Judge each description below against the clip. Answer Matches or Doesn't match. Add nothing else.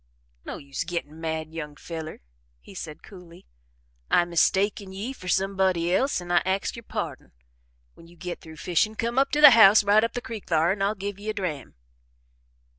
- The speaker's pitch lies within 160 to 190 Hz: Matches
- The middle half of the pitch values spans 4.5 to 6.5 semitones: Doesn't match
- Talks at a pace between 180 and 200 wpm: Matches